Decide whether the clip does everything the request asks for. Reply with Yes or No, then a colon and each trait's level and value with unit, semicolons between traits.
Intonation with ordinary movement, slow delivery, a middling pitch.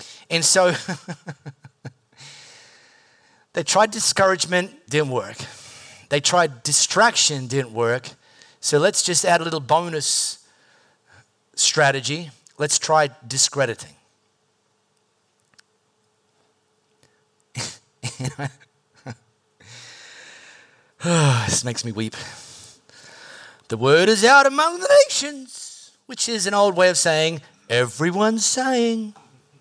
No: wide, 6.9 semitones; slow, 85 wpm; medium, 155 Hz